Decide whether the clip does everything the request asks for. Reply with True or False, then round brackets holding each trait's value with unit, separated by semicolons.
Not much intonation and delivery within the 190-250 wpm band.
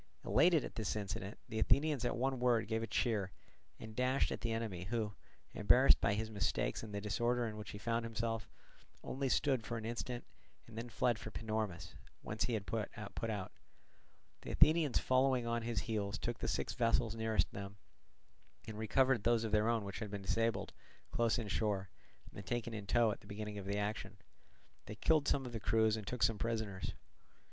True (2.2 semitones; 195 wpm)